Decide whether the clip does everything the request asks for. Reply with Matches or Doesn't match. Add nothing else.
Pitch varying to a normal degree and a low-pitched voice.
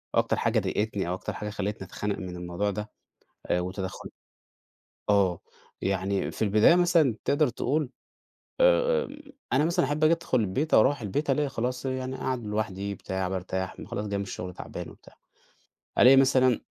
Doesn't match